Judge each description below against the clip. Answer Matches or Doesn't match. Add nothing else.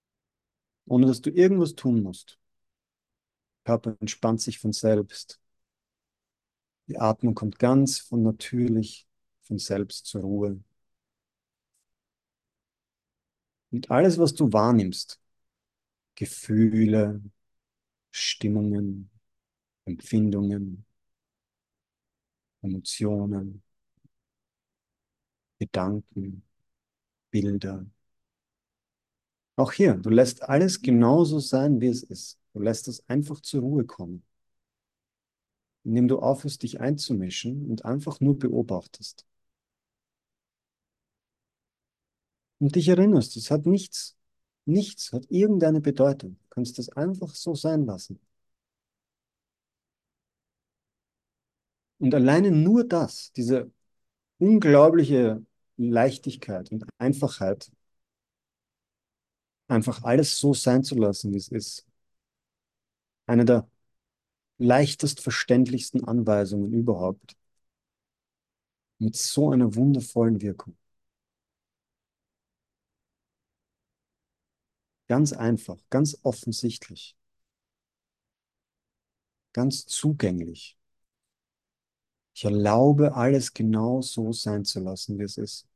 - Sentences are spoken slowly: Matches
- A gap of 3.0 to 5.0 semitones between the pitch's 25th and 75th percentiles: Matches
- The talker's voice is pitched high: Doesn't match